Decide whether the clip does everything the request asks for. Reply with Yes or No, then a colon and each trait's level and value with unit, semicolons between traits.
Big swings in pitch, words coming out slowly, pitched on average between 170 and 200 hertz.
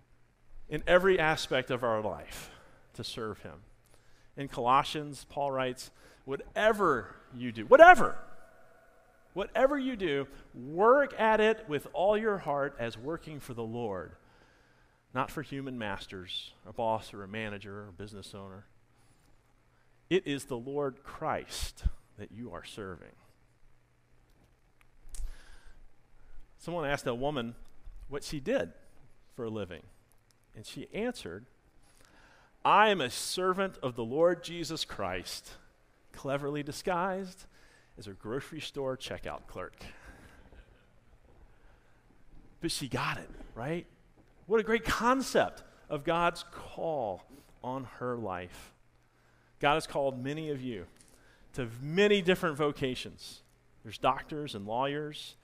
No: wide, 6.6 semitones; slow, 120 wpm; low, 130 Hz